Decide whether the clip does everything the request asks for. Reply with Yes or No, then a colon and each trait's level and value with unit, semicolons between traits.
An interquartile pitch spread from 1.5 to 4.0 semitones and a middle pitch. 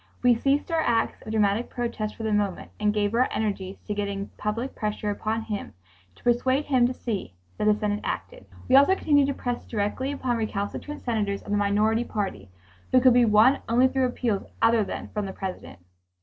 No: average, 3.3 semitones; high, 220 Hz